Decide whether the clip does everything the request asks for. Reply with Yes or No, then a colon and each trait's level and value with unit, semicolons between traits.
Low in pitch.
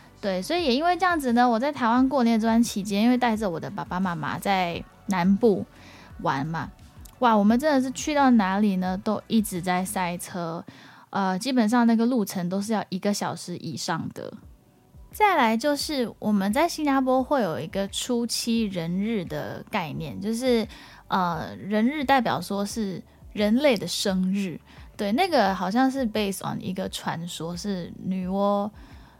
No: high, 210 Hz